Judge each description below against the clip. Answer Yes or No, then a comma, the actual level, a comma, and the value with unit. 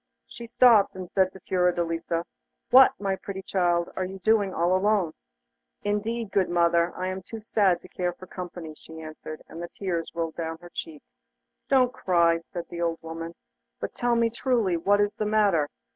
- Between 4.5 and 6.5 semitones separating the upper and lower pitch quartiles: No, average, 3.4 semitones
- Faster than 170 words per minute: Yes, average, 180 wpm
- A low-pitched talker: No, medium, 180 Hz